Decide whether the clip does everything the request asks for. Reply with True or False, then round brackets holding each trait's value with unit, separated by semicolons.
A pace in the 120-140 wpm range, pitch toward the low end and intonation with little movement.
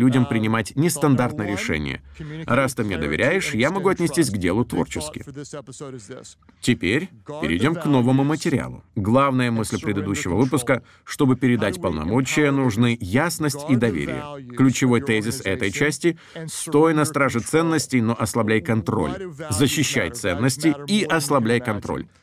False (125 wpm; 130 Hz; 4.8 semitones)